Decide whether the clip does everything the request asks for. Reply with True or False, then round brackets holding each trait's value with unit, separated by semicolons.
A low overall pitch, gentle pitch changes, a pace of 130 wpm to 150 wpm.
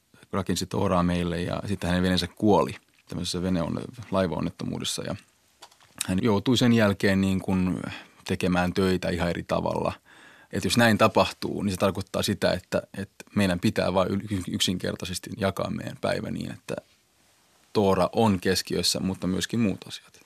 True (95 Hz; 1.9 semitones; 145 wpm)